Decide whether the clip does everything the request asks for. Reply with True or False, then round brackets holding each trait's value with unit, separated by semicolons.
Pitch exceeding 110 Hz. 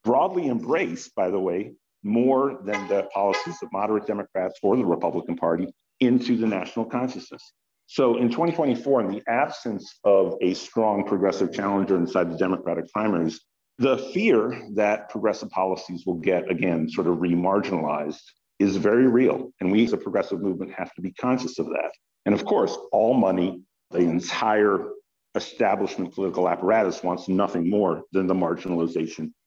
False (100 Hz)